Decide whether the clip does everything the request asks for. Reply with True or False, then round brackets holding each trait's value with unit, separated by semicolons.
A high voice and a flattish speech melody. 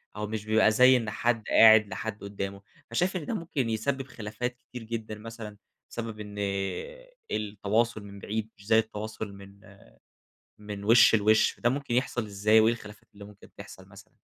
False (110 Hz; 2.0 semitones)